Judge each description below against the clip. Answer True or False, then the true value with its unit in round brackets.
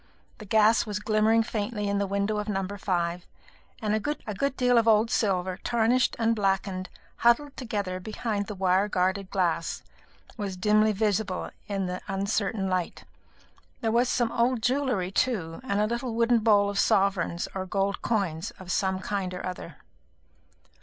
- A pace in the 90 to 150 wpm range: False (160 wpm)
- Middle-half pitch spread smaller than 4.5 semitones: True (3.0 semitones)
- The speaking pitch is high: True (205 Hz)